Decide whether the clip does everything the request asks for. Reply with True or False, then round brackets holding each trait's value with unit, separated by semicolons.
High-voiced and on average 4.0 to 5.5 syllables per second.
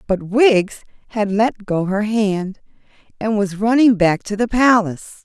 True (210 Hz; 4.2 syllables/s)